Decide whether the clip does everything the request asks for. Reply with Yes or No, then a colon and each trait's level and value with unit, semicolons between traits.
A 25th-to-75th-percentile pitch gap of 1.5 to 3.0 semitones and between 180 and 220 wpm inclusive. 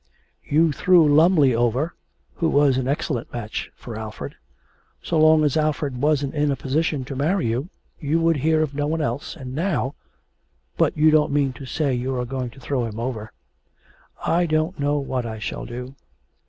No: average, 3.7 semitones; average, 185 wpm